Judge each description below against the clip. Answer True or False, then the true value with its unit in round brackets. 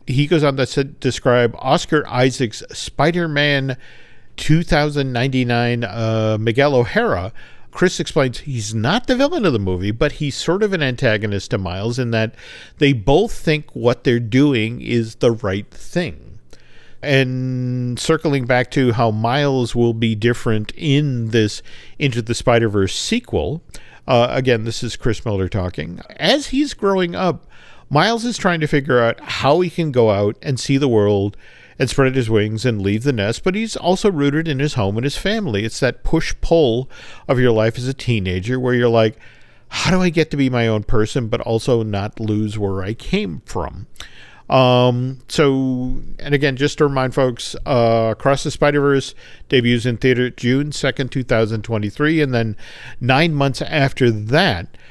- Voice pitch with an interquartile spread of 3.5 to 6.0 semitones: True (4.1 semitones)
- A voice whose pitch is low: True (130 Hz)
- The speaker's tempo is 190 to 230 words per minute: False (170 wpm)